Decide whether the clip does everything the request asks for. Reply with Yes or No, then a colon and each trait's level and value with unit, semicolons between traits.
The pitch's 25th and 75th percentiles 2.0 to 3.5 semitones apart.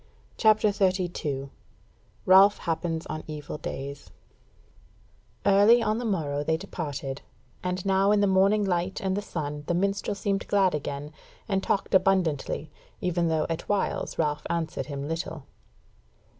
No: average, 4.5 semitones